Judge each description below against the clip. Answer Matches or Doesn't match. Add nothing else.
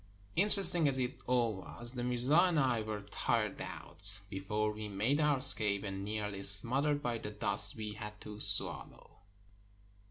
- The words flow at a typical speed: Matches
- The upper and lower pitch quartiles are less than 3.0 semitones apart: Doesn't match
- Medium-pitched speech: Doesn't match